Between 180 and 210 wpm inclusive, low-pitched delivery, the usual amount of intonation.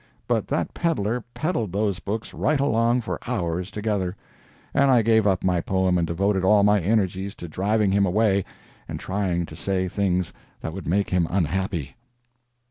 No: average, 170 wpm; low, 100 Hz; average, 3.0 semitones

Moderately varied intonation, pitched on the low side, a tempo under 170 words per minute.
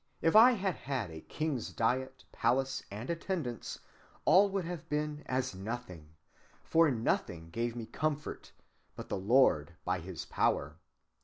No: wide, 7.3 semitones; low, 130 Hz; average, 145 wpm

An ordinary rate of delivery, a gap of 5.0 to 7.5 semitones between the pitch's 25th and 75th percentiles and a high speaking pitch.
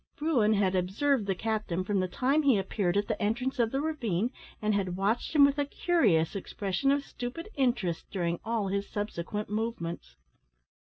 Yes: average, 175 wpm; wide, 5.6 semitones; high, 215 Hz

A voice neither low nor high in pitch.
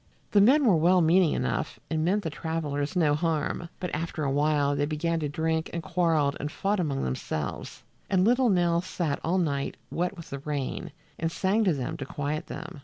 Yes: medium, 160 Hz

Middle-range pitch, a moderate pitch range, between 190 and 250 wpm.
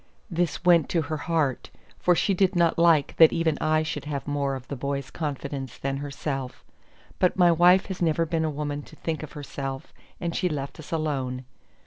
Yes: medium, 155 Hz; average, 3.2 semitones; average, 195 wpm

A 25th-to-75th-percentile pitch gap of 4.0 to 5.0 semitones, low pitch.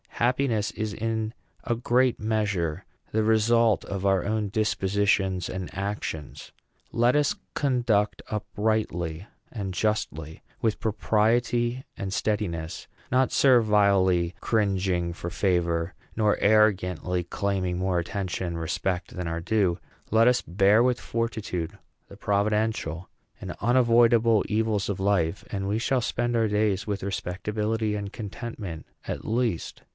No: average, 3.3 semitones; low, 105 Hz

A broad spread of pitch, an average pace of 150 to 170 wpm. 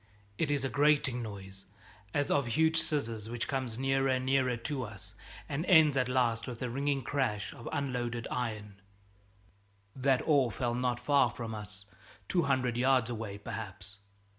No: average, 3.2 semitones; average, 165 wpm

